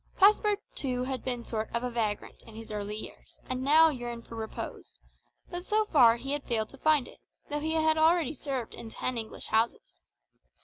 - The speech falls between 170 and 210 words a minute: Yes, average, 190 wpm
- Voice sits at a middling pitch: No, very high, 255 Hz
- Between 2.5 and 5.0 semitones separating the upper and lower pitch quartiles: No, wide, 5.5 semitones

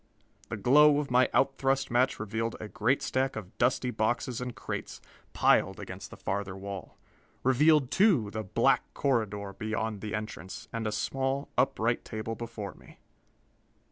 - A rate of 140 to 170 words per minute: Yes, average, 155 wpm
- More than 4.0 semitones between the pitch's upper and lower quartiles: No, average, 3.7 semitones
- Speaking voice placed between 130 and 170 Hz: No, low, 115 Hz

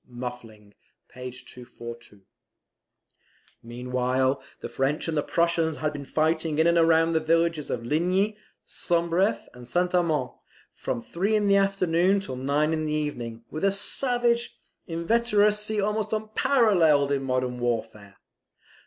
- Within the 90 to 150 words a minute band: Yes, slow, 135 wpm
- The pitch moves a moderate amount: No, wide, 7.0 semitones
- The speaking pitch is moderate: Yes, medium, 160 Hz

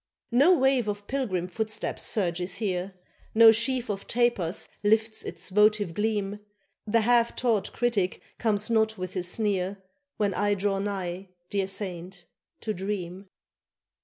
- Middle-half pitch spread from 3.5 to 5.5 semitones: No, average, 2.9 semitones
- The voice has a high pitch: Yes, high, 205 Hz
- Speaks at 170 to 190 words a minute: No, slow, 135 wpm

